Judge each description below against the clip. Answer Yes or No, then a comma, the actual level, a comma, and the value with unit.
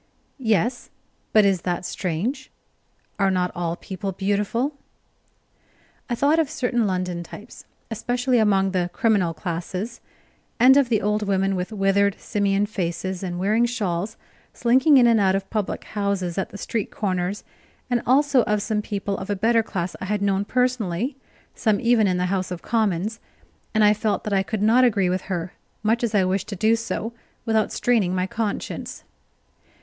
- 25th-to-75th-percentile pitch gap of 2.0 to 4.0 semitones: Yes, average, 3.5 semitones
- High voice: Yes, high, 205 Hz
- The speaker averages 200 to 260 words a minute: No, average, 170 wpm